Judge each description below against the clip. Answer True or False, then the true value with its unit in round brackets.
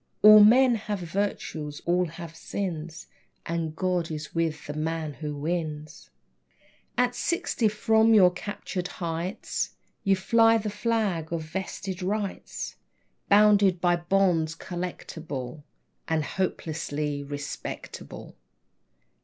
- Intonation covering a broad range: False (4.3 semitones)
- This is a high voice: False (175 Hz)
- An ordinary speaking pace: False (110 wpm)